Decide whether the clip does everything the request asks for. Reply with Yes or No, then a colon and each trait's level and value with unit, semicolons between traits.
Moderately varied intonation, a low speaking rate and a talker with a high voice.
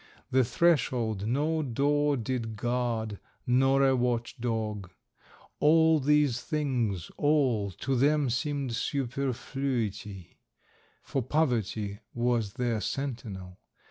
No: average, 3.9 semitones; slow, 100 wpm; low, 125 Hz